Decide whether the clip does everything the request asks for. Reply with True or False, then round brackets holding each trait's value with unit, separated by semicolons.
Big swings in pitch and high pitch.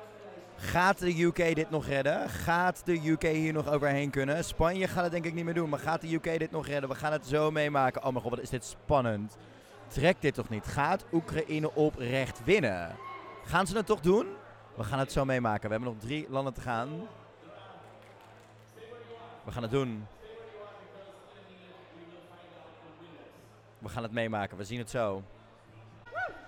False (6.3 semitones; 140 Hz)